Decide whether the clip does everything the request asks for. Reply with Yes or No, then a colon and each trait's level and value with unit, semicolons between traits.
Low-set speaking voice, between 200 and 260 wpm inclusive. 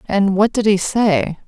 No: high, 205 Hz; fast, 205 wpm